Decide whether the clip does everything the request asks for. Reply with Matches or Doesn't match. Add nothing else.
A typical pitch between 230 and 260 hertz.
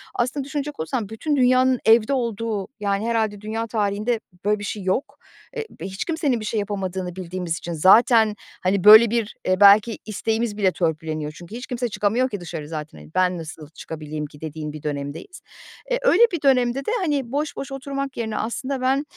Doesn't match